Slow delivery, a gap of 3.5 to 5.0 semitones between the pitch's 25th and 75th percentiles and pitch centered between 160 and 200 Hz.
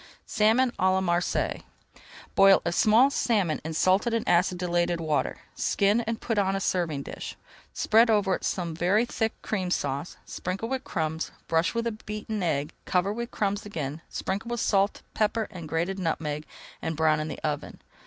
No: average, 170 wpm; average, 4.7 semitones; high, 190 Hz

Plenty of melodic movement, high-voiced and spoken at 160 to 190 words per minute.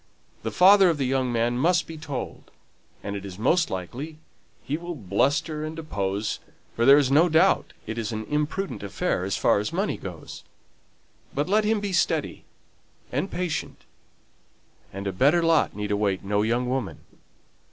No: wide, 8.1 semitones; low, 135 Hz; average, 170 wpm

